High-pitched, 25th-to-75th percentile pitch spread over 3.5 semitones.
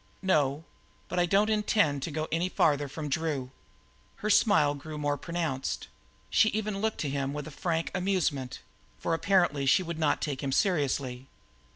No: medium, 155 Hz; average, 4.6 semitones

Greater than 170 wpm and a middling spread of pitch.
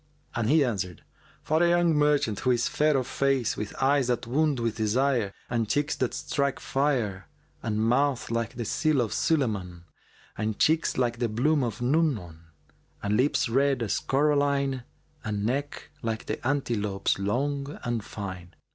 No: average, 160 wpm; average, 4.6 semitones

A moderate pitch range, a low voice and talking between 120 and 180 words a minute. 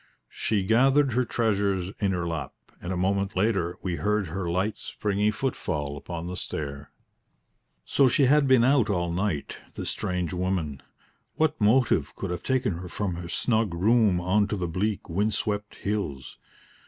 Yes: average, 3.9 semitones; low, 100 Hz; average, 165 wpm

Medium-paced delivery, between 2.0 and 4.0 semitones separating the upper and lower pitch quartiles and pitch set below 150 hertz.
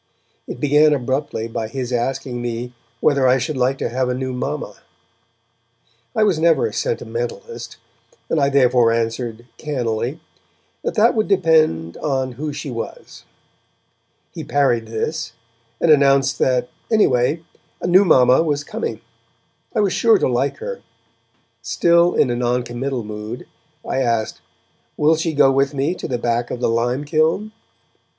No: average, 150 wpm; average, 4.5 semitones; low, 135 Hz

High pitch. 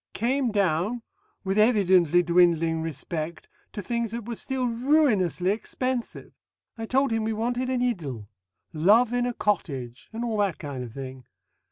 Yes: high, 210 Hz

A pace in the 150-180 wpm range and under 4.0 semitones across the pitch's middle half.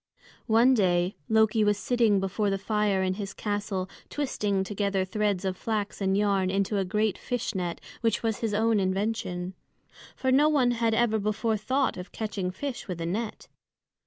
Yes: average, 175 wpm; average, 2.8 semitones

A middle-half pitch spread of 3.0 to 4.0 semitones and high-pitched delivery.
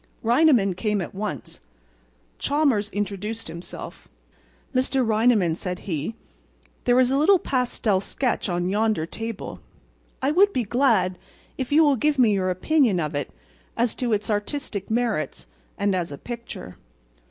No: average, 5.3 semitones; high, 220 Hz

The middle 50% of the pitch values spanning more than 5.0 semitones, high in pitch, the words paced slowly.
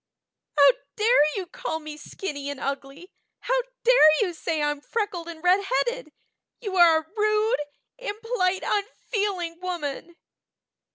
Yes: wide, 5.5 semitones; very high, 360 Hz; slow, 125 wpm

